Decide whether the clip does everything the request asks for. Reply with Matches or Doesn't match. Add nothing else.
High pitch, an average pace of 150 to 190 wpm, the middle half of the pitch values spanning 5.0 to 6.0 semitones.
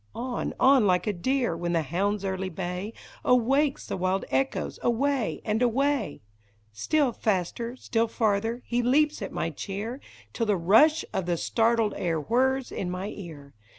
Matches